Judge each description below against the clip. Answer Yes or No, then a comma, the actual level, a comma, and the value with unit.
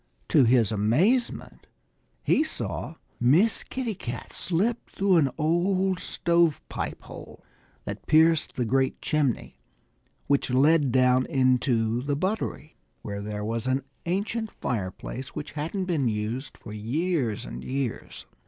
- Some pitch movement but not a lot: No, wide, 6.3 semitones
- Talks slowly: Yes, slow, 130 wpm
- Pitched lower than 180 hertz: Yes, medium, 140 Hz